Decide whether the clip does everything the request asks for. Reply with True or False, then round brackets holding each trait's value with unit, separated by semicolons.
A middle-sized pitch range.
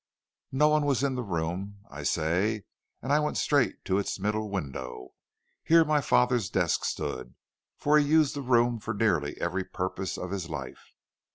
False (7.6 semitones)